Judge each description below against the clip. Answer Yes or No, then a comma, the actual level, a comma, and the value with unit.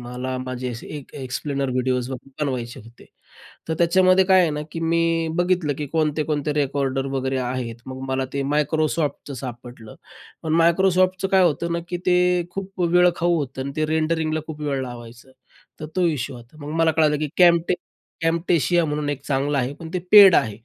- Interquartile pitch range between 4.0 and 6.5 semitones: Yes, average, 4.4 semitones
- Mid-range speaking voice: Yes, medium, 150 Hz